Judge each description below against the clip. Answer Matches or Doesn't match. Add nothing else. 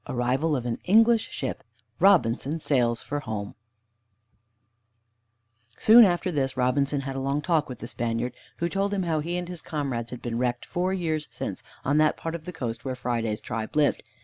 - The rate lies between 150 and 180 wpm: Doesn't match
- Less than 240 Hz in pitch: Matches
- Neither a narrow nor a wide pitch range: Doesn't match